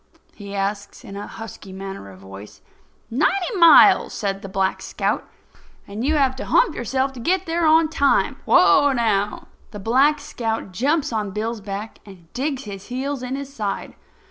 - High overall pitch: Yes, high, 230 Hz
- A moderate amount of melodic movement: No, wide, 6.0 semitones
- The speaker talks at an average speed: Yes, average, 170 wpm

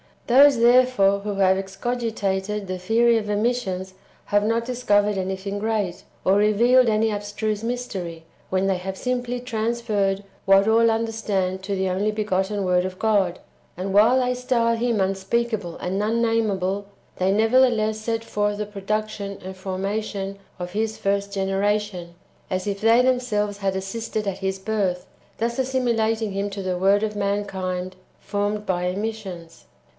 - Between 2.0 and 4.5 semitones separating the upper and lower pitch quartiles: Yes, average, 2.8 semitones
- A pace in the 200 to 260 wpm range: No, average, 155 wpm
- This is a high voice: Yes, high, 205 Hz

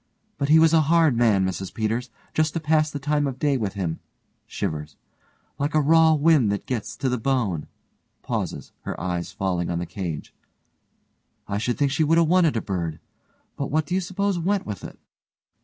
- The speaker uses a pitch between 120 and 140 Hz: Yes, low, 135 Hz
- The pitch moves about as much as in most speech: No, wide, 8.1 semitones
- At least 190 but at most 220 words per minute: Yes, average, 195 wpm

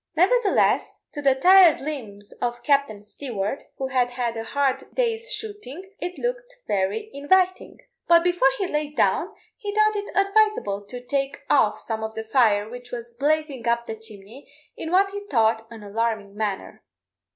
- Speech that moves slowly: No, average, 165 wpm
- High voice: Yes, very high, 270 Hz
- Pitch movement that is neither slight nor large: No, wide, 8.7 semitones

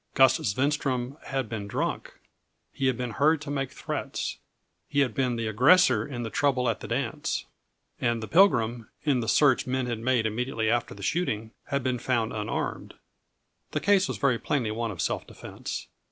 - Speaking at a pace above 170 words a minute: Yes, average, 180 wpm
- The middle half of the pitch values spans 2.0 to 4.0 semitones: Yes, average, 3.5 semitones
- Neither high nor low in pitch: No, low, 125 Hz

